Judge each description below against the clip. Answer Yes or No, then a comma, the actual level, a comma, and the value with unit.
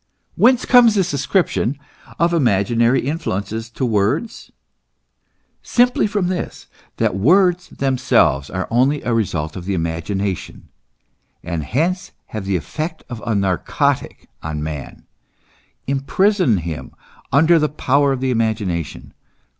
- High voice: No, low, 125 Hz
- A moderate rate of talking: No, slow, 120 wpm